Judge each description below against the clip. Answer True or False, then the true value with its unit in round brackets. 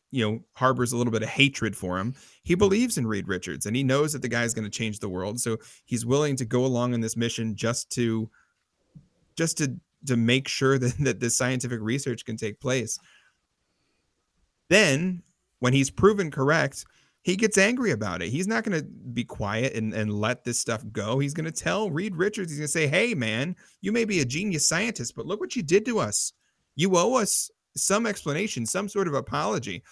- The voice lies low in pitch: True (130 Hz)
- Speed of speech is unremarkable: False (215 wpm)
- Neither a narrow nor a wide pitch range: False (7.2 semitones)